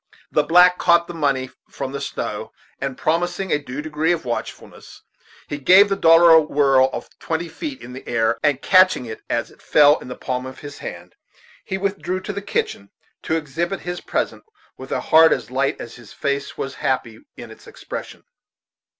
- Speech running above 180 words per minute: Yes, average, 195 wpm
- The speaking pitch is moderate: Yes, medium, 150 Hz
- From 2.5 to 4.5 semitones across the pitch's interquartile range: No, average, 4.9 semitones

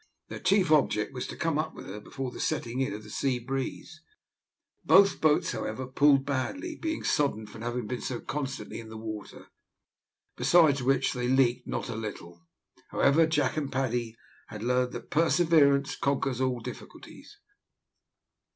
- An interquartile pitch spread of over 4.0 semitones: No, average, 3.7 semitones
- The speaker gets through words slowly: No, average, 160 wpm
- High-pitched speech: No, low, 130 Hz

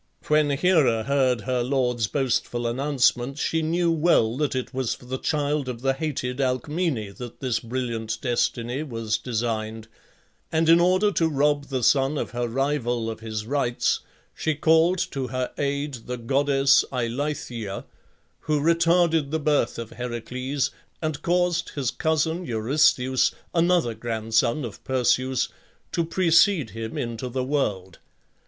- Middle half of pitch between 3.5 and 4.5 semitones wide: Yes, average, 4.2 semitones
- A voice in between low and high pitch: No, low, 130 Hz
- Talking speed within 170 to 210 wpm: No, average, 145 wpm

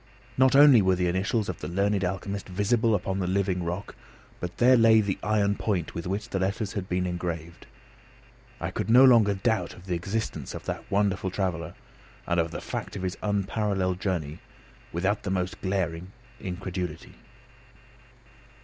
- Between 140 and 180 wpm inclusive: Yes, average, 165 wpm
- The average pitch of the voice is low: Yes, very low, 95 Hz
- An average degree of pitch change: No, narrow, 2.3 semitones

